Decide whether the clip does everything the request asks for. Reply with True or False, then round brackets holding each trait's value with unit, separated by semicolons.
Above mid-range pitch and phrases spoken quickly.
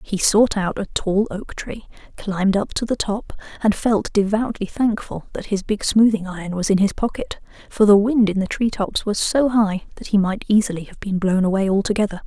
True (205 Hz; 215 wpm)